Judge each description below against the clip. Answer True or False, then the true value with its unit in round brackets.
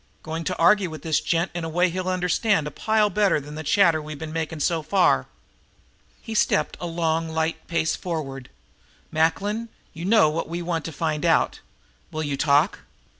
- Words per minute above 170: True (185 wpm)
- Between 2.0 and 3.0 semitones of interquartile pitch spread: True (2.5 semitones)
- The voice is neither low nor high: True (165 Hz)